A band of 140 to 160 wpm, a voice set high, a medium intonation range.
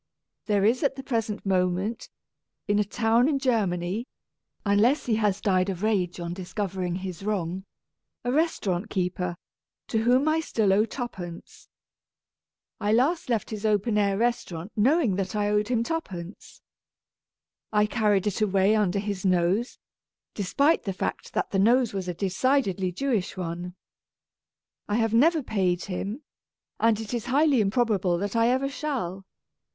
Yes: average, 150 wpm; high, 210 Hz; average, 4.1 semitones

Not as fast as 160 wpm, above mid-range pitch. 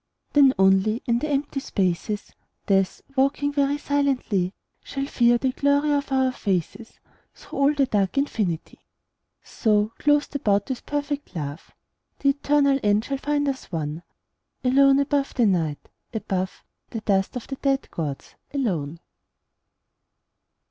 Yes: slow, 135 wpm; very high, 255 Hz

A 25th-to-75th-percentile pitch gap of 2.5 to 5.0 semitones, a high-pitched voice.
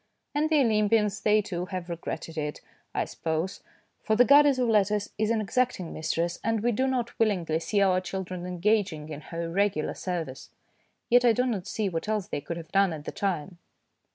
Yes: average, 4.6 semitones; high, 195 Hz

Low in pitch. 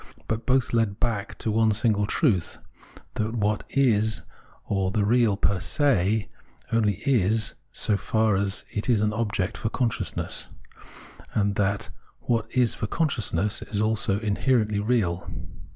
Yes: low, 110 Hz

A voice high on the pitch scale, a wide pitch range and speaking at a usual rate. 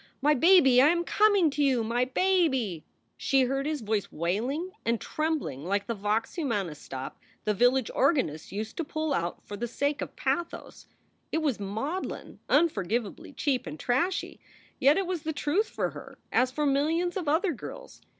Yes: very high, 275 Hz; wide, 6.5 semitones; average, 180 wpm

